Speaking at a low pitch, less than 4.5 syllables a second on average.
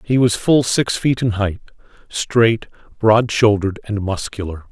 Yes: low, 110 Hz; 4.3 syllables/s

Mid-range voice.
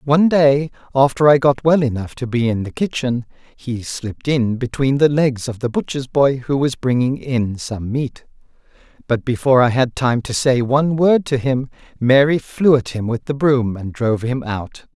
No: low, 130 Hz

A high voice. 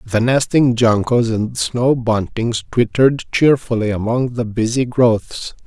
No: low, 120 Hz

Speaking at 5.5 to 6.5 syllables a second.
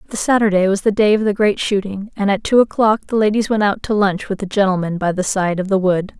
Yes: 6.0 syllables/s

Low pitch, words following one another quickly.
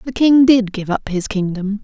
No: high, 215 Hz; fast, 230 wpm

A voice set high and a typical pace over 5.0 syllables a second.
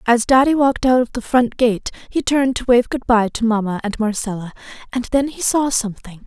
Yes: high, 240 Hz; 5.7 syllables/s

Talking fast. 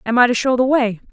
Yes: fast, 320 wpm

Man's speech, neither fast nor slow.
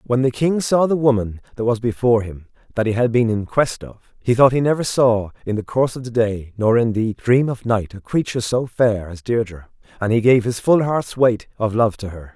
No: male; fast, 250 wpm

